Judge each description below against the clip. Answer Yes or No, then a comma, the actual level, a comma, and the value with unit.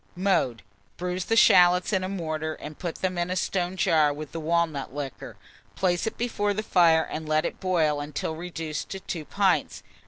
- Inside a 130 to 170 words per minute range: No, average, 190 wpm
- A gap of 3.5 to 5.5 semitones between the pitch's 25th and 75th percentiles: No, average, 3.1 semitones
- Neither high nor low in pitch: Yes, medium, 170 Hz